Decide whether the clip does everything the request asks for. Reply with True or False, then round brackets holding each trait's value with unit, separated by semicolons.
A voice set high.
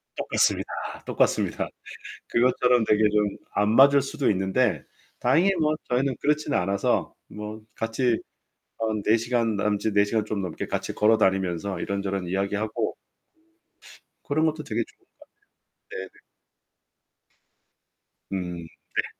False (110 Hz)